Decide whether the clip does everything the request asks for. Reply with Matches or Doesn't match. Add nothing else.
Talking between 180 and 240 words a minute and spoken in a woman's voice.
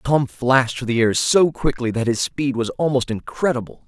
Doesn't match